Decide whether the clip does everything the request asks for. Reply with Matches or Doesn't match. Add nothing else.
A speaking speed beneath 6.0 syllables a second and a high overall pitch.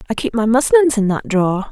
Doesn't match